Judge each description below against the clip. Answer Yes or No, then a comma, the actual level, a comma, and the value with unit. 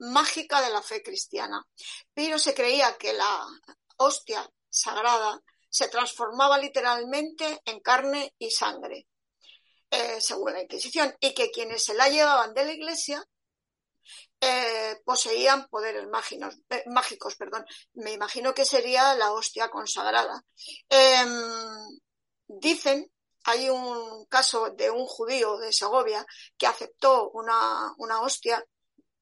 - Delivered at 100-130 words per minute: Yes, slow, 125 wpm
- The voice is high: Yes, very high, 265 Hz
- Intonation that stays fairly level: No, average, 4.6 semitones